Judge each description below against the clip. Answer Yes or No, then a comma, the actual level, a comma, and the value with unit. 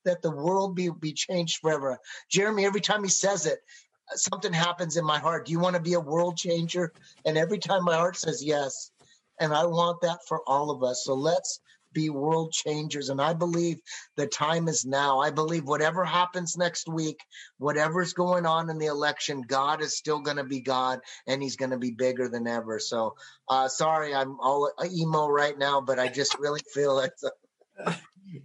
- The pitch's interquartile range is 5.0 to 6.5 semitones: No, average, 3.8 semitones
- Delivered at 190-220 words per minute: Yes, average, 200 wpm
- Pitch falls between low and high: Yes, medium, 155 Hz